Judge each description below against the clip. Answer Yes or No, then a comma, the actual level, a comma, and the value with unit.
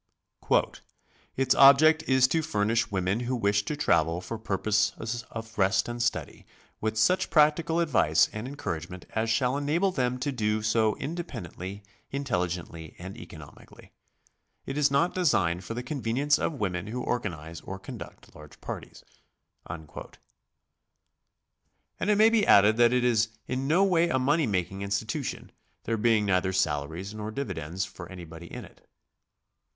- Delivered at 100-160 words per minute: Yes, average, 150 wpm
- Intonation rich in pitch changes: Yes, wide, 6.7 semitones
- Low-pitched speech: Yes, low, 110 Hz